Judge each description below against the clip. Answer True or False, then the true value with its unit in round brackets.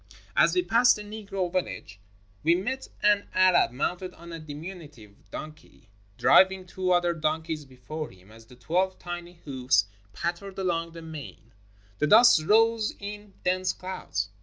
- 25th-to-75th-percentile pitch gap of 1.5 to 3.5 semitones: False (4.0 semitones)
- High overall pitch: False (175 Hz)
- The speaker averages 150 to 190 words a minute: True (155 wpm)